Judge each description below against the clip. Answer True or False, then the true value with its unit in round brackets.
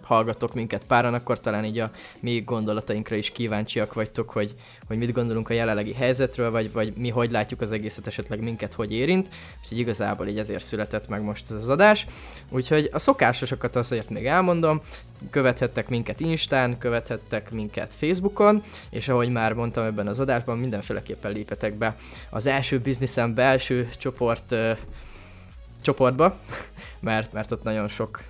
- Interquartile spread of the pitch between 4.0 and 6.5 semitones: False (2.8 semitones)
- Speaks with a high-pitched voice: False (115 Hz)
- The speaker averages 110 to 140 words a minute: False (155 wpm)